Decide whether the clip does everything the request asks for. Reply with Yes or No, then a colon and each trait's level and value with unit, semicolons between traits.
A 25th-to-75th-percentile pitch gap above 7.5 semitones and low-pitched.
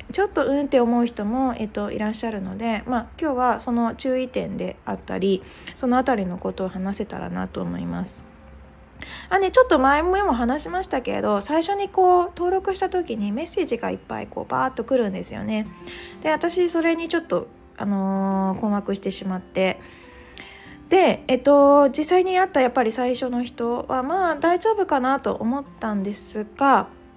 No: wide, 7.9 semitones; very high, 250 Hz